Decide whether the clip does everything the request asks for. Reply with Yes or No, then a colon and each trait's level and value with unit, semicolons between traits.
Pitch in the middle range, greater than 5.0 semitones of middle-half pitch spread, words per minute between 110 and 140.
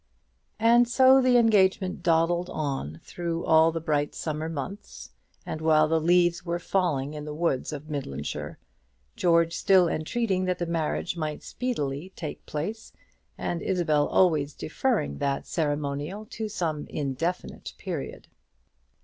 No: medium, 165 Hz; average, 3.6 semitones; slow, 135 wpm